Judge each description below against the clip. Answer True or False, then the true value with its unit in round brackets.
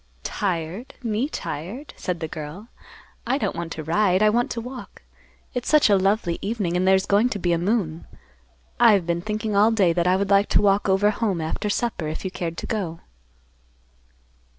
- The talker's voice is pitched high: True (195 Hz)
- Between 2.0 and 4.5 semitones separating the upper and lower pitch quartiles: True (4.1 semitones)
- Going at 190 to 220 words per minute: True (195 wpm)